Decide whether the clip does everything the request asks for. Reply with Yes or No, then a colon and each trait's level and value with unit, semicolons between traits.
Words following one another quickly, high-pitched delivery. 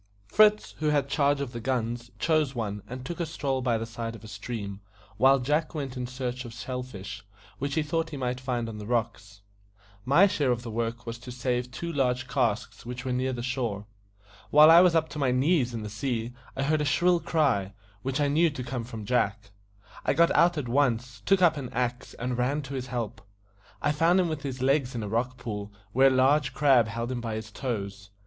No: fast, 225 wpm; low, 125 Hz